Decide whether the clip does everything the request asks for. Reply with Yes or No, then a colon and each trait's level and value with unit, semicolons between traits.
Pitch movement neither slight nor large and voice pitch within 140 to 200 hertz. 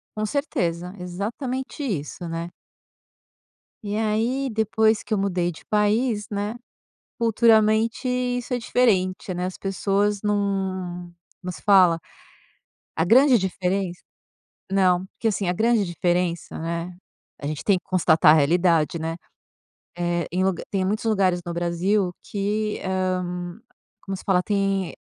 Yes: average, 3.3 semitones; high, 190 Hz